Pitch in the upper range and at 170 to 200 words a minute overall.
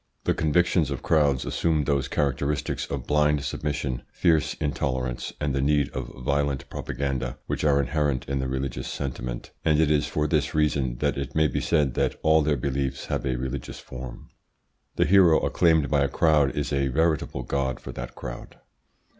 No: very low, 70 Hz; average, 180 wpm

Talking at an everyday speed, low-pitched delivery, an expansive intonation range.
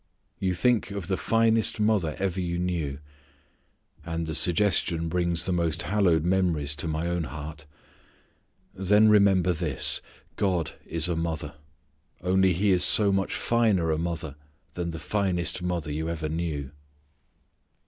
No: average, 145 wpm; very low, 85 Hz; average, 2.9 semitones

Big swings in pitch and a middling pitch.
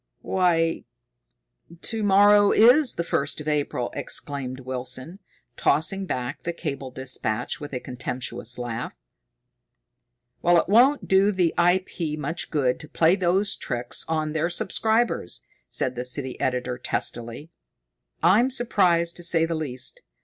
Yes: wide, 6.5 semitones; medium, 160 Hz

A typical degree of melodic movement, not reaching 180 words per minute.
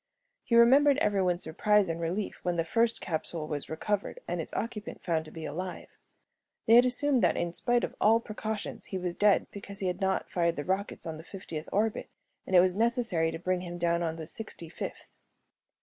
No: average, 4.5 semitones; fast, 205 wpm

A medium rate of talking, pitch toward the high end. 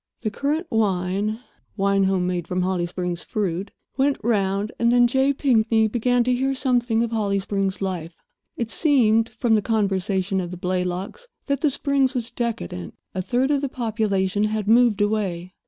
Yes: average, 170 wpm; high, 215 Hz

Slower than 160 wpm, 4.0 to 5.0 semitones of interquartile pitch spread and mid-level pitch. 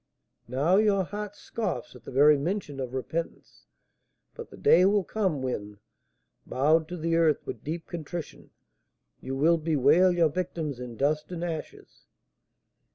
Yes: average, 150 wpm; average, 4.4 semitones; medium, 160 Hz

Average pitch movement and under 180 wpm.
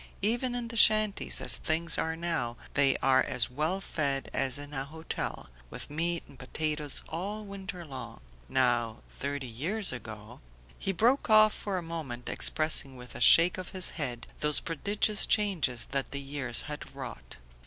No: wide, 6.1 semitones; average, 170 wpm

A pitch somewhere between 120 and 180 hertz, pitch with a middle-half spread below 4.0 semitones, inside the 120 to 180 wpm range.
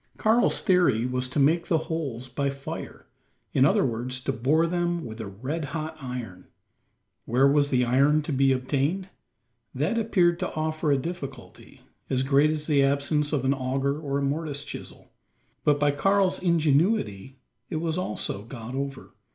Yes: medium, 140 Hz; average, 3.6 semitones; average, 165 wpm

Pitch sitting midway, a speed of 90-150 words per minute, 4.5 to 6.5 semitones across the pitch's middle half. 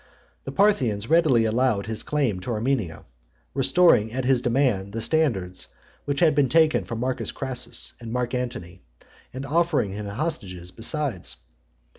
No: low, 125 Hz; average, 145 wpm; average, 4.9 semitones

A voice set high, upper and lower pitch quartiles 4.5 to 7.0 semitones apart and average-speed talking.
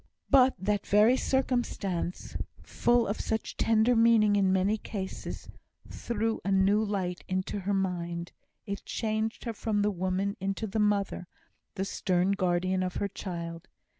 No: high, 200 Hz; average, 2.8 semitones; average, 145 wpm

